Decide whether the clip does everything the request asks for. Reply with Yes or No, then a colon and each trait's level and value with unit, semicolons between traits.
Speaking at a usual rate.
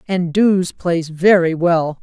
Yes: average, 150 wpm